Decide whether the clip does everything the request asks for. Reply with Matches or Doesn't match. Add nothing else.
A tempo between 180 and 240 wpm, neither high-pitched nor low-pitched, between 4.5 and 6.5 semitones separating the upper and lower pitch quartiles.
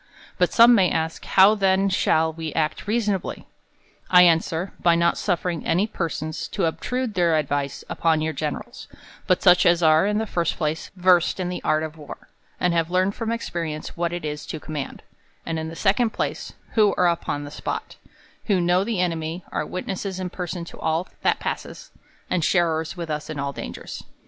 Doesn't match